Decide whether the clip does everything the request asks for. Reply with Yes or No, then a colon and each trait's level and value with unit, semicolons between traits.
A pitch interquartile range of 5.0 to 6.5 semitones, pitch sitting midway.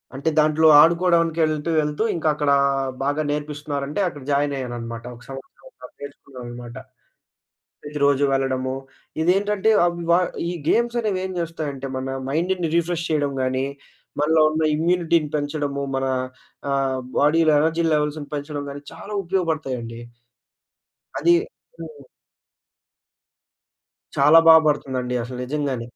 No: average, 3.3 semitones; medium, 150 Hz